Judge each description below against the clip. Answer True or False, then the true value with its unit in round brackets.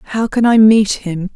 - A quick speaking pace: True (220 wpm)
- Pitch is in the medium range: False (210 Hz)